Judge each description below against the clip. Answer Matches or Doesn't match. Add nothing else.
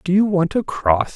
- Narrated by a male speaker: Matches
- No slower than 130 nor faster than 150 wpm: Doesn't match